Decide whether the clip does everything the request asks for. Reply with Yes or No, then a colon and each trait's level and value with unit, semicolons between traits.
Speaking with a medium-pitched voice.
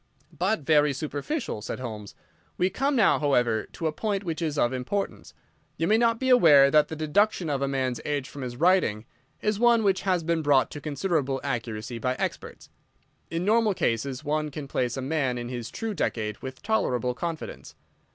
Yes: medium, 150 Hz